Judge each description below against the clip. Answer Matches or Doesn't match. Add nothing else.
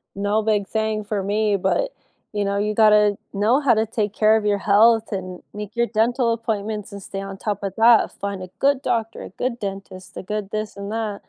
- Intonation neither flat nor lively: Doesn't match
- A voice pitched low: Doesn't match